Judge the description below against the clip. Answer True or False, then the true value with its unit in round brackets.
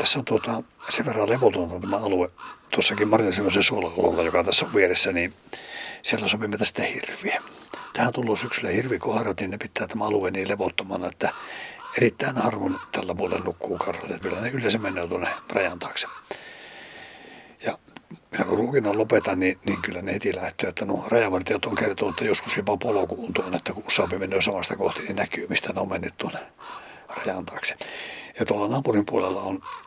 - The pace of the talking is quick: True (170 wpm)